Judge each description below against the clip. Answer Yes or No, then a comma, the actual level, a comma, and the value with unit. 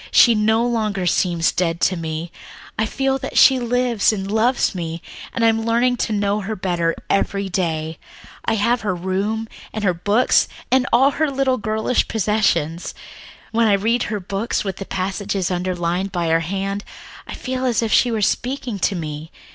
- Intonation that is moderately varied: Yes, average, 4.2 semitones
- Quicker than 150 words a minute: Yes, average, 180 wpm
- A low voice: No, high, 205 Hz